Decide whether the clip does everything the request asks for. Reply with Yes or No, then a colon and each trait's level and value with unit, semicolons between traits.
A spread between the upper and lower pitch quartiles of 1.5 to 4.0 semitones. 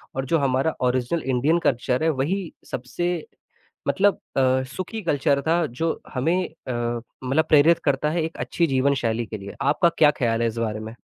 No: average, 4.7 semitones